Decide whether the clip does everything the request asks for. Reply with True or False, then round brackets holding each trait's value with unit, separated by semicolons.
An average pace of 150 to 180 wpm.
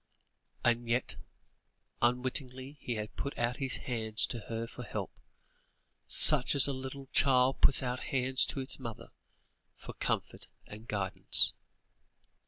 False (135 wpm)